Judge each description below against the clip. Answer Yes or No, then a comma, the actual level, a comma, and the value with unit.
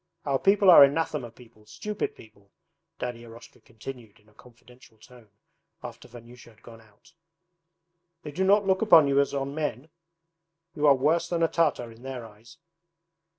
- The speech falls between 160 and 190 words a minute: Yes, average, 165 wpm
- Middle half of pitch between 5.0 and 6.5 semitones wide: Yes, wide, 5.4 semitones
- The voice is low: Yes, low, 130 Hz